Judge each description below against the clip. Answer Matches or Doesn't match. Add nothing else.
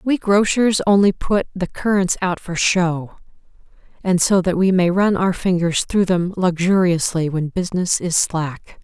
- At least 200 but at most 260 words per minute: Doesn't match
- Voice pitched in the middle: Matches